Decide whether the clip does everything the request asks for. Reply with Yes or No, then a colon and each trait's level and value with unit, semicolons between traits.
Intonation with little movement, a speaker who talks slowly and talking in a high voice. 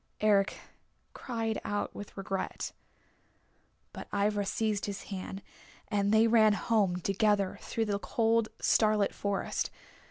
Yes: narrow, 1.6 semitones; slow, 120 wpm; high, 205 Hz